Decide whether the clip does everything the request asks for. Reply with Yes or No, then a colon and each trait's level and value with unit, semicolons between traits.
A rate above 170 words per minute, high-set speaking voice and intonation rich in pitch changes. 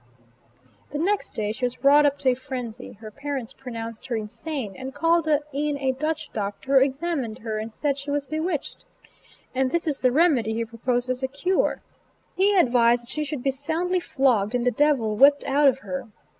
No: average, 200 wpm; very high, 270 Hz; average, 3.8 semitones